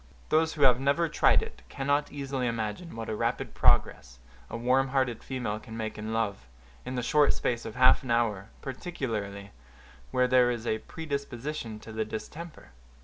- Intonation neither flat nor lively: Yes, average, 4.0 semitones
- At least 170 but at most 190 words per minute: Yes, average, 175 wpm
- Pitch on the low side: Yes, low, 125 Hz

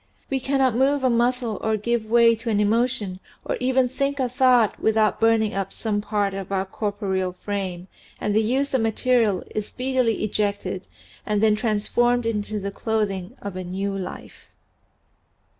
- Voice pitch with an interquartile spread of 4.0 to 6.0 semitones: No, average, 3.3 semitones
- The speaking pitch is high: Yes, high, 220 Hz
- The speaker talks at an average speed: Yes, average, 170 wpm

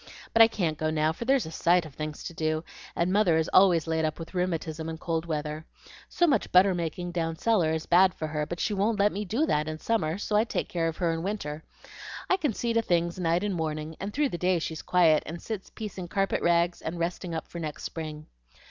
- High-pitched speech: No, medium, 170 Hz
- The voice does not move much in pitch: No, average, 3.5 semitones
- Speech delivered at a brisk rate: Yes, fast, 245 wpm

